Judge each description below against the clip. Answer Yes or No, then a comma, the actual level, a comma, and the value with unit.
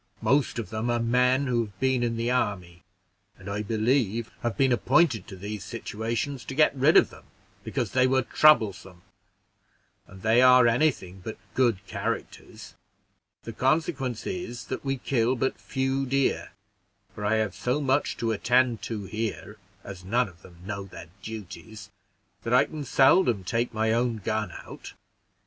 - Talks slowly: No, average, 165 wpm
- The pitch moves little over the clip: No, average, 3.7 semitones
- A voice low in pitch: Yes, low, 115 Hz